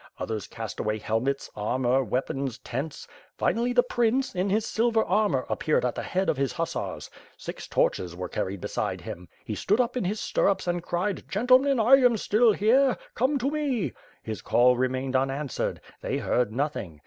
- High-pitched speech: No, medium, 170 Hz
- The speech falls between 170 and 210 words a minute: Yes, average, 175 wpm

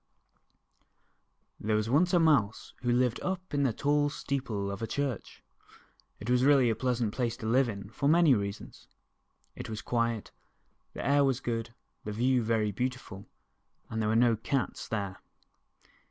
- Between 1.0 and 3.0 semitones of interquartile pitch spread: No, average, 4.0 semitones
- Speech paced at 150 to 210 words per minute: Yes, average, 170 wpm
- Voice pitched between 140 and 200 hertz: No, low, 120 Hz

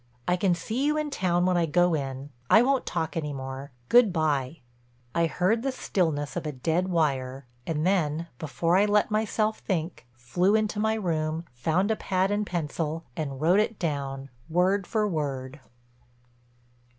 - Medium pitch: Yes, medium, 170 Hz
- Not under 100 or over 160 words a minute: No, average, 170 wpm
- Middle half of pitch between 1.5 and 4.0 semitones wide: No, average, 5.3 semitones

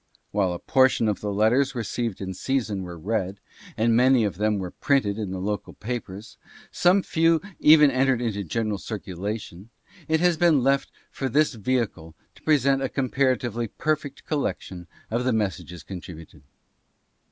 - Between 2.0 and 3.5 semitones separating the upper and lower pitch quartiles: No, average, 5.3 semitones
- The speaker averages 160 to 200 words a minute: Yes, average, 165 wpm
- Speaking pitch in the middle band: No, low, 115 Hz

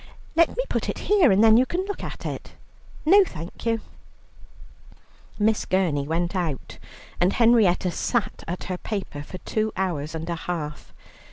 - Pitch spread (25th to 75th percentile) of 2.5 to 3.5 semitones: No, average, 5.3 semitones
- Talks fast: No, average, 165 wpm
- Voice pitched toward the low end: No, high, 190 Hz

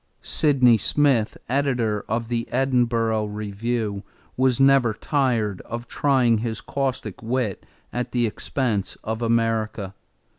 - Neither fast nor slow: No, slow, 115 wpm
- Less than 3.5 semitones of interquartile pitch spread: Yes, average, 2.9 semitones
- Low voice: Yes, low, 115 Hz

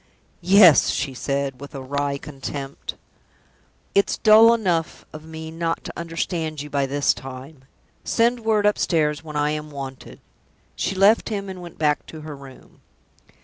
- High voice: No, medium, 155 Hz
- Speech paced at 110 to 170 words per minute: Yes, average, 155 wpm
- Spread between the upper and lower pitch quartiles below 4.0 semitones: No, average, 4.7 semitones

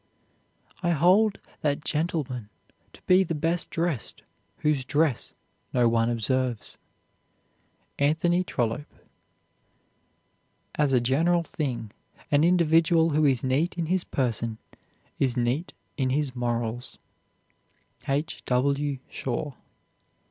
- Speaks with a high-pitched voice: No, medium, 145 Hz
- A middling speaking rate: No, slow, 105 wpm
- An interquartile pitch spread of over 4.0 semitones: Yes, average, 4.7 semitones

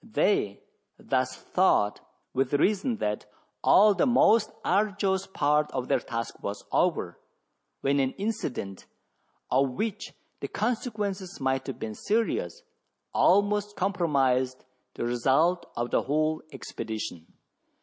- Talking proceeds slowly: Yes, slow, 120 wpm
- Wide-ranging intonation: Yes, wide, 8.0 semitones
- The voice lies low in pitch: No, medium, 155 Hz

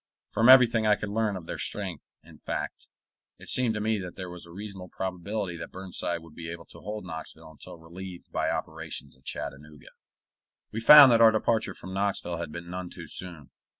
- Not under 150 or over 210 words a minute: Yes, average, 200 wpm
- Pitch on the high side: No, very low, 95 Hz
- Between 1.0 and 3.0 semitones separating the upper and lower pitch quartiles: No, average, 4.1 semitones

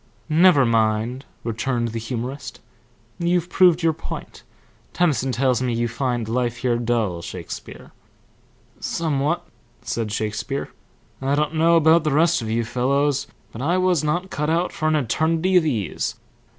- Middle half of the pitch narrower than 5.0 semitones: No, wide, 5.5 semitones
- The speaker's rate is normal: Yes, average, 150 wpm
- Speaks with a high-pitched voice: No, low, 135 Hz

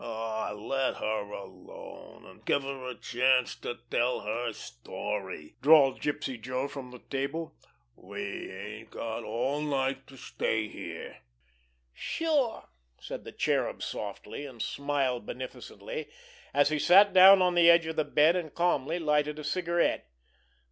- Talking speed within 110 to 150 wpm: Yes, average, 145 wpm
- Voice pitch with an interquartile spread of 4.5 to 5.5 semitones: Yes, average, 5.2 semitones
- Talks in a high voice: No, low, 135 Hz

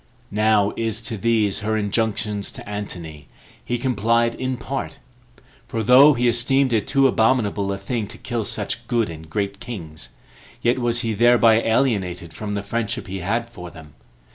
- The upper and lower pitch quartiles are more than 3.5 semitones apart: No, average, 2.9 semitones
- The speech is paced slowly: No, average, 165 wpm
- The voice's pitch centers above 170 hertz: No, low, 110 Hz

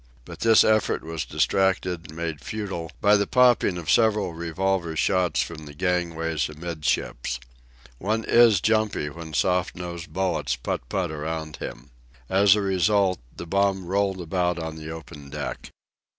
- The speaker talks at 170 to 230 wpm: No, average, 150 wpm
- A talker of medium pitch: No, very low, 90 Hz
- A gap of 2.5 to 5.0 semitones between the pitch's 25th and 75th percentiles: Yes, average, 3.4 semitones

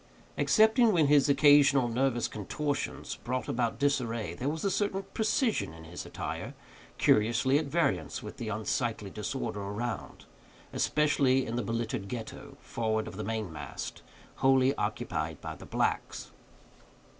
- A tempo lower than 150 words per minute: Yes, average, 140 wpm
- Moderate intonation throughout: Yes, average, 4.9 semitones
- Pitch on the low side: Yes, low, 120 Hz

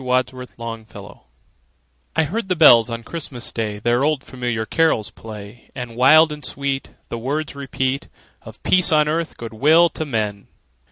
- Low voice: Yes, low, 130 Hz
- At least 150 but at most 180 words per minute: Yes, average, 160 wpm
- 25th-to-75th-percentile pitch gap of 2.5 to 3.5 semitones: No, average, 4.8 semitones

